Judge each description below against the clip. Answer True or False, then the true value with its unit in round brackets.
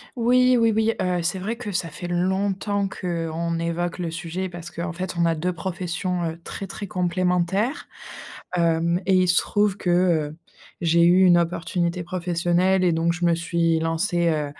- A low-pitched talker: False (175 Hz)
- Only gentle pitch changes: True (1.8 semitones)